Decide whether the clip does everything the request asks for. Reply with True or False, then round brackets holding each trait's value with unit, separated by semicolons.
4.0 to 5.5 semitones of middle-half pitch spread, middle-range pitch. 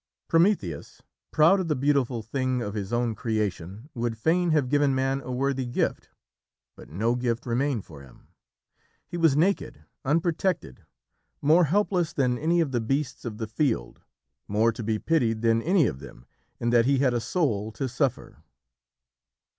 False (5.1 semitones; 125 Hz)